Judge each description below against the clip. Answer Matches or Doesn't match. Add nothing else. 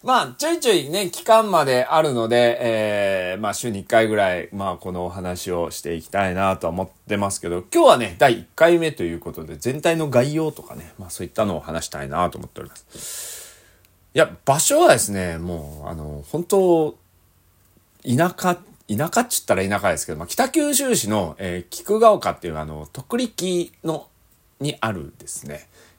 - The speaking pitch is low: Matches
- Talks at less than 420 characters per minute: Matches